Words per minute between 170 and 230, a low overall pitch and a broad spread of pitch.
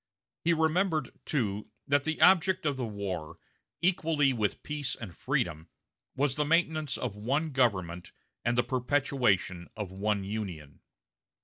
No: slow, 135 wpm; low, 125 Hz; wide, 7.0 semitones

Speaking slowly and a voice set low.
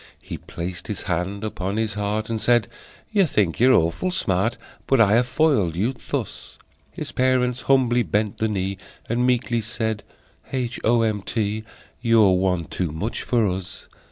No: average, 165 wpm; low, 110 Hz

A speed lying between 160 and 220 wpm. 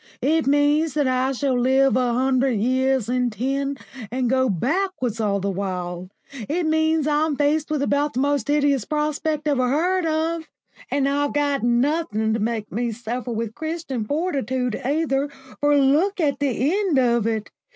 Yes: average, 165 wpm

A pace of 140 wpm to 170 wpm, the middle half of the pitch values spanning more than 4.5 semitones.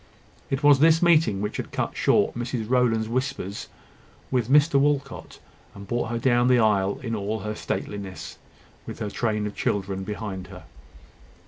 No: average, 160 wpm; average, 4.1 semitones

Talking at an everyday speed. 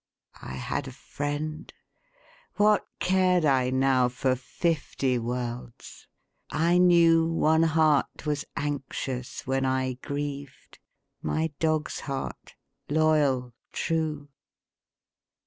No: slow, 95 wpm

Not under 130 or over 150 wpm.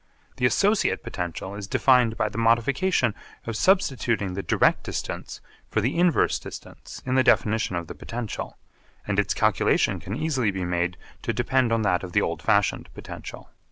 No: average, 170 wpm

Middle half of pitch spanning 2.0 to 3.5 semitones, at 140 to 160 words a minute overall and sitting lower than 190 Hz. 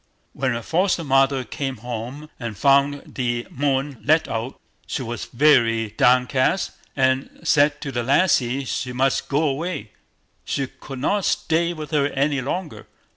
Yes: average, 2.9 semitones; average, 150 wpm; low, 135 Hz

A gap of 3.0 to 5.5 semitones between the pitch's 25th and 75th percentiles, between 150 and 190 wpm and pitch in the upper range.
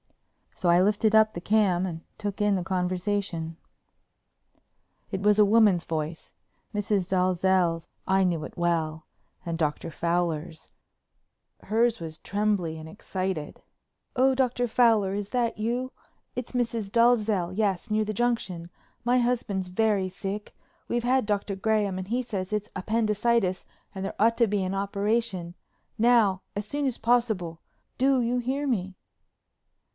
No: average, 4.0 semitones; average, 140 wpm; high, 205 Hz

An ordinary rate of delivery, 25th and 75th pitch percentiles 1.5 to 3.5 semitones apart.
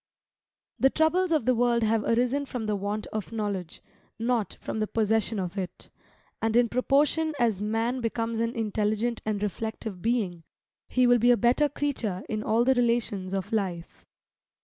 Yes: average, 170 wpm; average, 2.7 semitones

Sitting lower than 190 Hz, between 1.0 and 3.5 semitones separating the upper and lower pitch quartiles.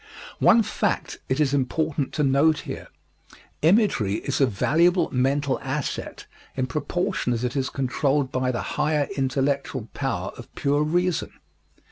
Yes: medium, 140 Hz; average, 2.9 semitones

